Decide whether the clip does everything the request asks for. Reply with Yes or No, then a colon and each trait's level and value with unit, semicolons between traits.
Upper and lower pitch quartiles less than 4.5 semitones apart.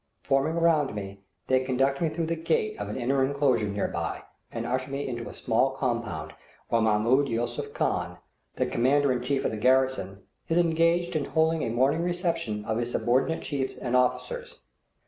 No: average, 5.2 semitones